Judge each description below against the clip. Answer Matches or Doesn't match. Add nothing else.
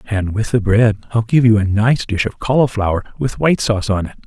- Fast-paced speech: Matches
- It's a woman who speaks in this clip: Doesn't match